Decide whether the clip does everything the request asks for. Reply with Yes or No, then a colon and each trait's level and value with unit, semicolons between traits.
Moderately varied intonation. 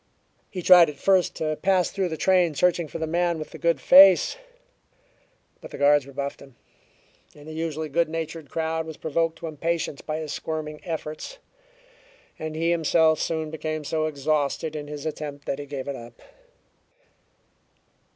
No: narrow, 2.0 semitones